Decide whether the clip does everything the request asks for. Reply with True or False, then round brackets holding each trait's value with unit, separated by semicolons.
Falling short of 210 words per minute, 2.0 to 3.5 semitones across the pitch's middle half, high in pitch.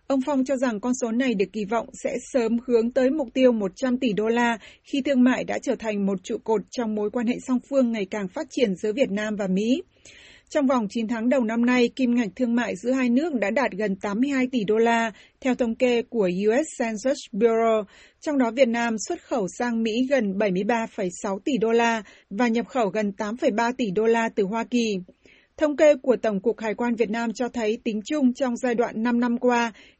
False (230 wpm; 2.7 semitones; 235 Hz)